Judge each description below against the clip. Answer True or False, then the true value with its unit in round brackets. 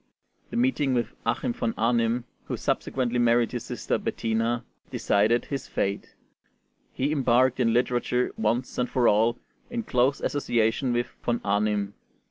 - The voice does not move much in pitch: True (2.1 semitones)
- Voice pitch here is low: True (120 Hz)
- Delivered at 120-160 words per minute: True (140 wpm)